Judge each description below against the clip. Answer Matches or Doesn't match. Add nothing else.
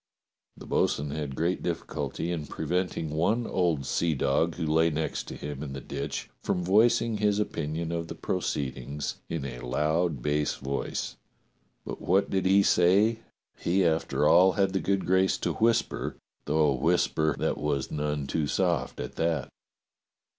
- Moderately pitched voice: Doesn't match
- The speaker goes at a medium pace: Matches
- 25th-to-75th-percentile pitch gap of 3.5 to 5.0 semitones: Matches